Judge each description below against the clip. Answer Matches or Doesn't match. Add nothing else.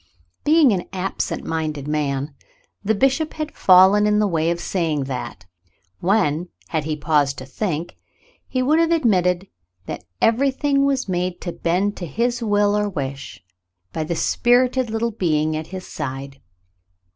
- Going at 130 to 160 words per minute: Matches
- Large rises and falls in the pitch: Matches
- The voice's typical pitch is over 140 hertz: Matches